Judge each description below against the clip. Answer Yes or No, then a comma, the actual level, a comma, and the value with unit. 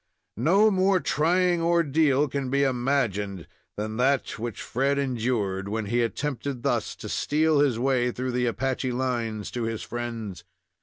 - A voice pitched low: Yes, low, 125 Hz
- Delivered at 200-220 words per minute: No, average, 150 wpm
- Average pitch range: Yes, average, 3.7 semitones